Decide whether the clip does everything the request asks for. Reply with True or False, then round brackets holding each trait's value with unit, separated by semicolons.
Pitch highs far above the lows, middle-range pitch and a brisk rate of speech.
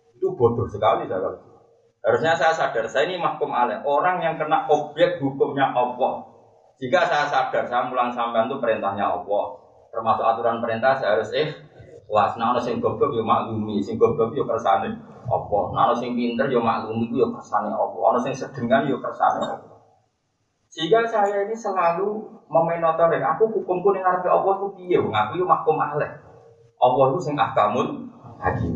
True (8.5 semitones; 155 Hz; 165 wpm)